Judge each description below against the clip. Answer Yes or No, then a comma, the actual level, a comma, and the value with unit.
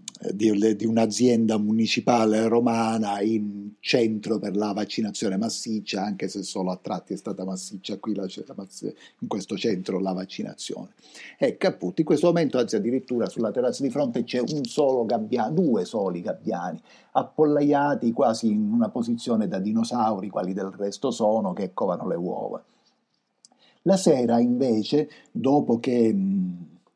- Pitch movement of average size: No, wide, 8.8 semitones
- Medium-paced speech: Yes, average, 145 wpm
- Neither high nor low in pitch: No, low, 115 Hz